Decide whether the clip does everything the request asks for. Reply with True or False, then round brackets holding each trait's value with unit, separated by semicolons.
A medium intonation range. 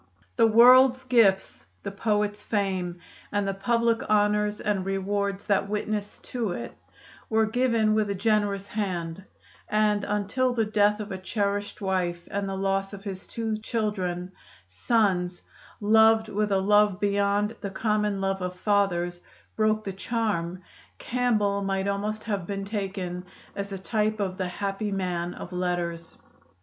False (1.9 semitones)